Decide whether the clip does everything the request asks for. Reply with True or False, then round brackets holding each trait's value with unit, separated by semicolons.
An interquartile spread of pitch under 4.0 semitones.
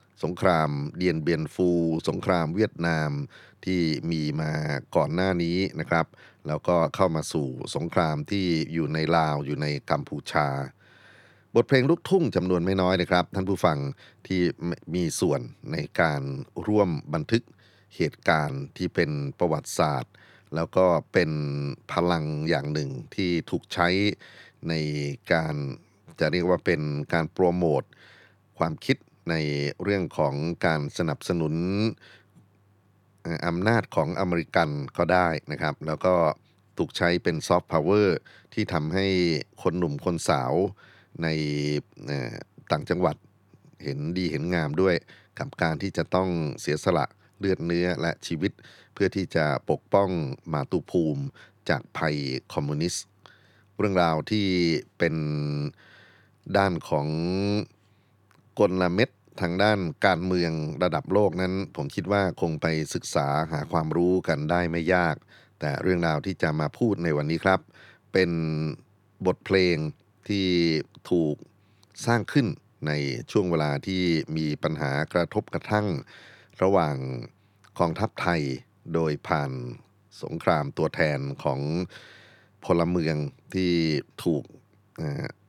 True (3.6 semitones)